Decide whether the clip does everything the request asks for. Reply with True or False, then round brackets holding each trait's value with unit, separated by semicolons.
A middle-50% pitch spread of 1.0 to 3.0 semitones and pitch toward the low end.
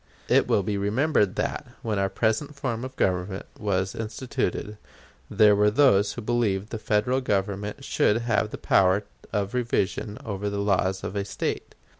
True (2.5 semitones; 105 Hz)